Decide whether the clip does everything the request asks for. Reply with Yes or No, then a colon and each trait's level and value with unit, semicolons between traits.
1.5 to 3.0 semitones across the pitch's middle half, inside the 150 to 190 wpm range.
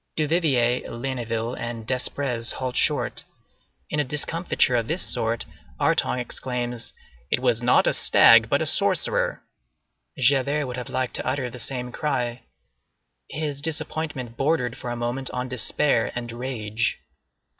No: average, 2.7 semitones; average, 140 wpm